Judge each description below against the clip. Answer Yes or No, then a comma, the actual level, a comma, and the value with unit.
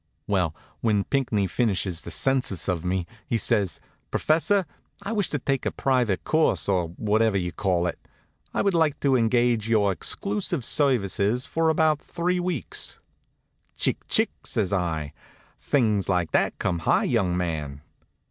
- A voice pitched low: Yes, low, 110 Hz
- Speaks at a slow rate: No, average, 150 wpm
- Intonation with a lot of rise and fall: Yes, wide, 7.3 semitones